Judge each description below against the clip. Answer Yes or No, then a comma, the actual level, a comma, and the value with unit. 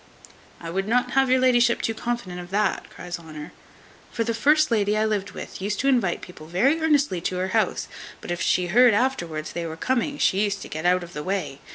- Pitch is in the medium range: No, high, 200 Hz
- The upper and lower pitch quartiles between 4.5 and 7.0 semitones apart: Yes, wide, 5.5 semitones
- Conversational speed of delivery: No, fast, 225 wpm